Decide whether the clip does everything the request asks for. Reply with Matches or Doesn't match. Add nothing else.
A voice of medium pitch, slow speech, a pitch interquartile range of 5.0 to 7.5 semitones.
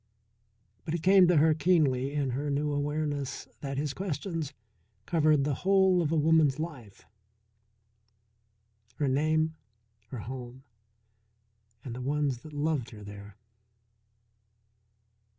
Doesn't match